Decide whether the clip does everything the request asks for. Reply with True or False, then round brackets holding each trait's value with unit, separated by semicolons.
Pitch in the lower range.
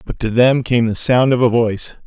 True (120 Hz)